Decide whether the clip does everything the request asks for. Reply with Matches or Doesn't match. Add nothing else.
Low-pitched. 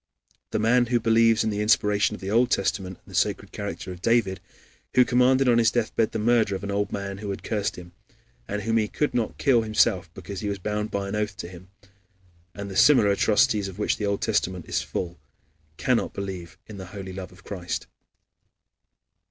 Matches